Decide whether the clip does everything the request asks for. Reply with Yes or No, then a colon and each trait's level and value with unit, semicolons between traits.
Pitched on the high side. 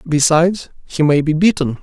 No: medium, 160 Hz